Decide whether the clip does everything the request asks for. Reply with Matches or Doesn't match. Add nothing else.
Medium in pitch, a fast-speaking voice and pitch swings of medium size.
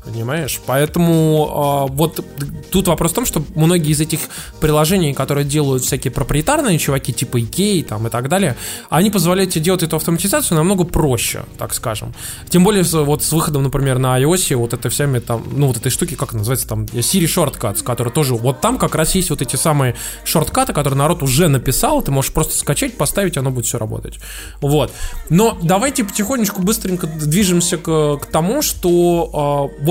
Matches